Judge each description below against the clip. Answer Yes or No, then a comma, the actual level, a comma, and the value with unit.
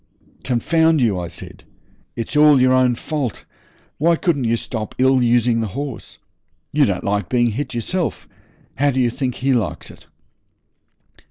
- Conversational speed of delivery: Yes, average, 160 wpm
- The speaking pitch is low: Yes, low, 125 Hz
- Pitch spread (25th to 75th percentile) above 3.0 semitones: Yes, average, 3.8 semitones